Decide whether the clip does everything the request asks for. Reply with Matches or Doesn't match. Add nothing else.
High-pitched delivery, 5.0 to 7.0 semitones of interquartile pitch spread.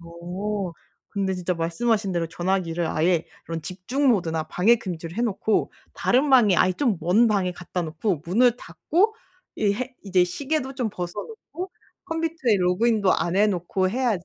Matches